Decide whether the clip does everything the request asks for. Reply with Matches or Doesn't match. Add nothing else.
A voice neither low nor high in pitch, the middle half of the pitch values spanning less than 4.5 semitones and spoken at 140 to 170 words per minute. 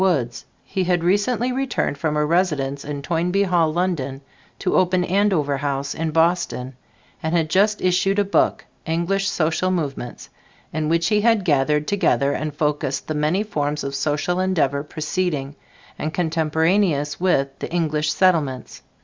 Matches